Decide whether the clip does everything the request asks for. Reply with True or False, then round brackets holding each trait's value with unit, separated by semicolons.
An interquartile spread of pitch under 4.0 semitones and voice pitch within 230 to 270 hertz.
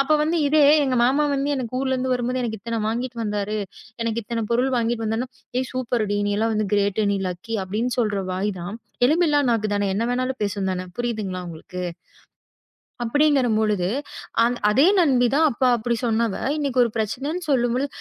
True (3.5 semitones; 235 Hz)